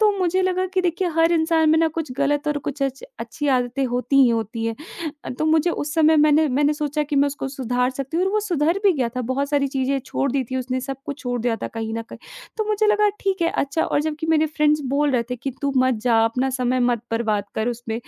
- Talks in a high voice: Yes, very high, 280 Hz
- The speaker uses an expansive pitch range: No, average, 4.3 semitones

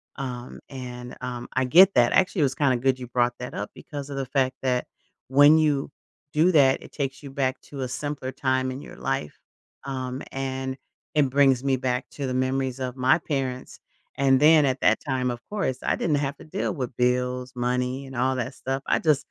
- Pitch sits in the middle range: No, low, 130 Hz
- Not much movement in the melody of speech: Yes, narrow, 1.7 semitones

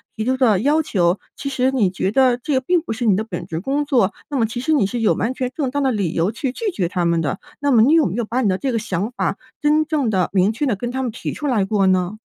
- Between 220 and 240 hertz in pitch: Yes, high, 235 Hz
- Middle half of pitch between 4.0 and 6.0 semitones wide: Yes, wide, 5.6 semitones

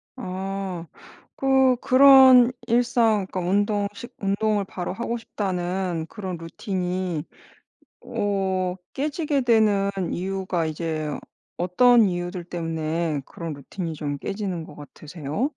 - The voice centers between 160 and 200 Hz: Yes, high, 190 Hz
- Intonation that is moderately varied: Yes, average, 4.5 semitones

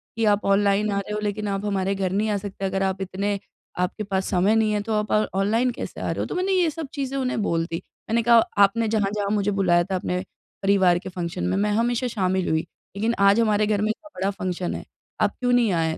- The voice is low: No, high, 205 Hz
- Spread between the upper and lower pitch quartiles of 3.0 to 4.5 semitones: No, narrow, 2.4 semitones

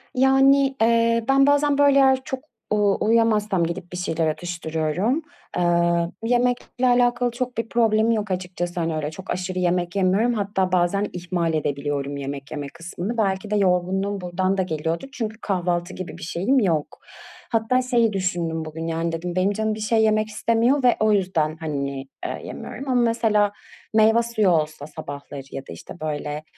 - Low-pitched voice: No, high, 190 Hz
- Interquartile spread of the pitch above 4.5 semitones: Yes, average, 5.3 semitones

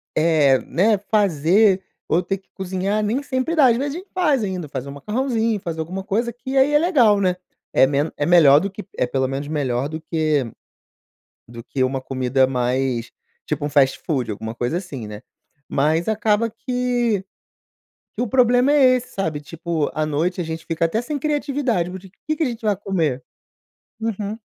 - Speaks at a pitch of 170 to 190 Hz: Yes, medium, 185 Hz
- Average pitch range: No, wide, 8.0 semitones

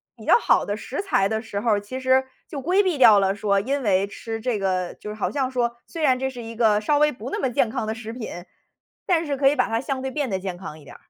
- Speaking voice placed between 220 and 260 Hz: Yes, high, 235 Hz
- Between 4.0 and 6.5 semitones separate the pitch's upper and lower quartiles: Yes, average, 4.5 semitones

